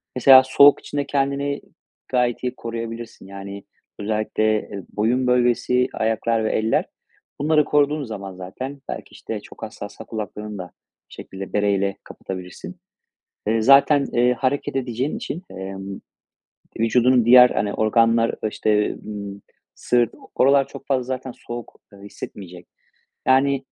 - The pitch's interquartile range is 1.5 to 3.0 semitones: No, average, 4.0 semitones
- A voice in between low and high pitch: No, low, 115 Hz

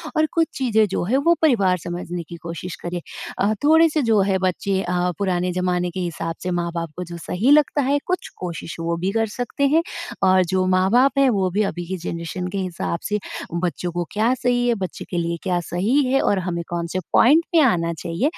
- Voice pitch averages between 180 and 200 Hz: Yes, medium, 185 Hz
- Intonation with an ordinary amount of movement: No, wide, 6.0 semitones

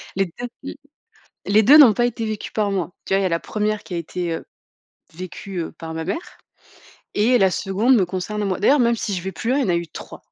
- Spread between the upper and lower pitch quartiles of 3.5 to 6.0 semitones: Yes, average, 4.1 semitones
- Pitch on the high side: Yes, high, 200 Hz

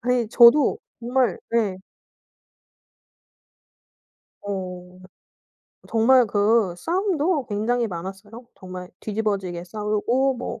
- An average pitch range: Yes, average, 4.2 semitones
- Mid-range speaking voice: No, high, 220 Hz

